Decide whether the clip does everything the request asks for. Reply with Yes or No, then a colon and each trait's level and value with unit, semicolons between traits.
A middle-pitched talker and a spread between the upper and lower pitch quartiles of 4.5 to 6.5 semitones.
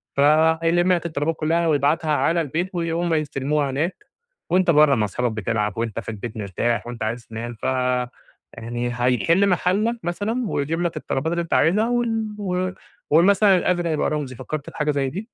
Yes: medium, 155 Hz; average, 5.2 semitones